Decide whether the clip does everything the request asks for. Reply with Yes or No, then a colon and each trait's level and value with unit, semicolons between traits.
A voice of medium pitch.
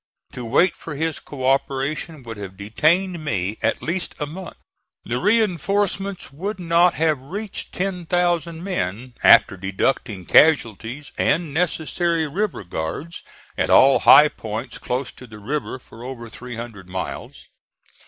Yes: medium, 145 Hz